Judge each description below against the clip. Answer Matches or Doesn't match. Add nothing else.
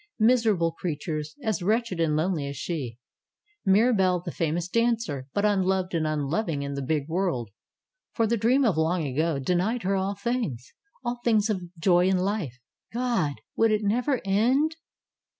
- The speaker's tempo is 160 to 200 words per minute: Matches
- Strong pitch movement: Matches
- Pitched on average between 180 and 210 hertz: Matches